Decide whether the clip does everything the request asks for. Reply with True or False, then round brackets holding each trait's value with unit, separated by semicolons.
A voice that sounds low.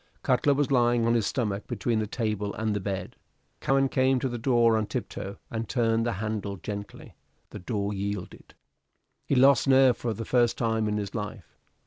True (115 Hz)